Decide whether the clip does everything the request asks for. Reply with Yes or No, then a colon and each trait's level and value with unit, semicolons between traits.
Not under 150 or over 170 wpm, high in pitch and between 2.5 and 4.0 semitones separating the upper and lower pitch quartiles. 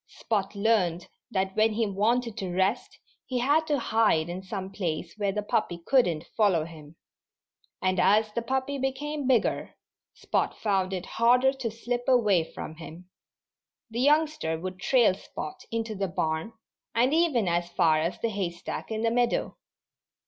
No: average, 165 wpm; high, 210 Hz; average, 5.2 semitones